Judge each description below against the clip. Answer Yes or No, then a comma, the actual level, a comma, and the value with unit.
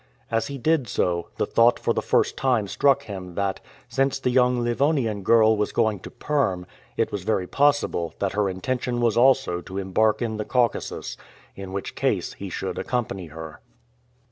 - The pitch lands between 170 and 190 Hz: No, low, 110 Hz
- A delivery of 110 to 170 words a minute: No, average, 180 wpm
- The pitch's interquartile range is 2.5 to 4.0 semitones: No, average, 4.7 semitones